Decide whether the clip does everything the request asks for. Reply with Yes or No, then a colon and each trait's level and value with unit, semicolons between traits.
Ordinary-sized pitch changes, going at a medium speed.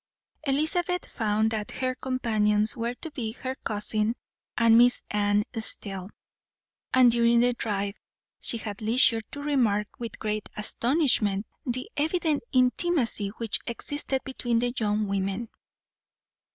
No: average, 3.5 semitones; slow, 125 wpm